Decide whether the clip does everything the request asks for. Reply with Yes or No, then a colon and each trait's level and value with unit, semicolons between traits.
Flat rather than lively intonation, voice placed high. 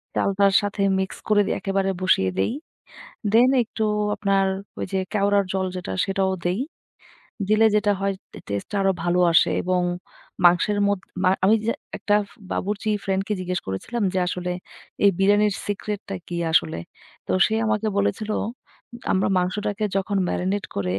Yes: narrow, 2.2 semitones; high, 195 Hz